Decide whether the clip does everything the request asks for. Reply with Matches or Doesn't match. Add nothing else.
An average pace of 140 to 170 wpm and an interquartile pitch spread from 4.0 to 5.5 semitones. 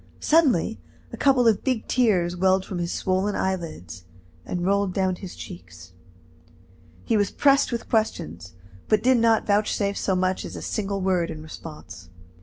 Matches